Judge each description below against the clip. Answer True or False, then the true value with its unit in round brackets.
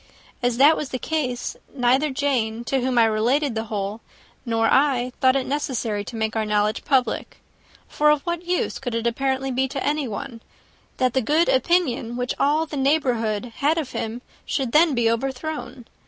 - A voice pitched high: True (255 Hz)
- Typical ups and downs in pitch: True (3.7 semitones)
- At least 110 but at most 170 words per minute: False (180 wpm)